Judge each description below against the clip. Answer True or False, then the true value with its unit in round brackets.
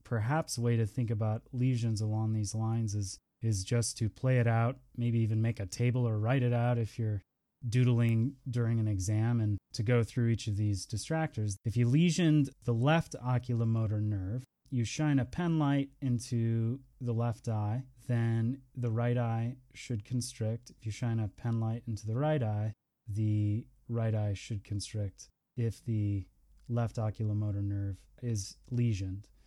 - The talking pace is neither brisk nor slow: True (170 wpm)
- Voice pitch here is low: True (115 Hz)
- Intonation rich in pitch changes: False (2.5 semitones)